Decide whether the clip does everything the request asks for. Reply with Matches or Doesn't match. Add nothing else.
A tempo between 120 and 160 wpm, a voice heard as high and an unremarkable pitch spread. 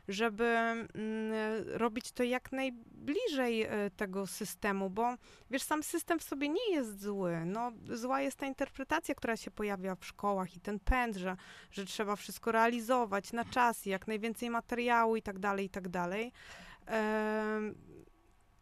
Matches